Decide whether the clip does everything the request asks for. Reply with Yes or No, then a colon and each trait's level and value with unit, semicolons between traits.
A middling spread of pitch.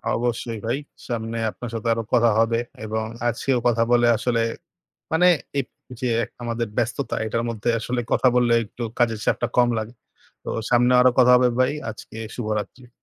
No: narrow, 1.4 semitones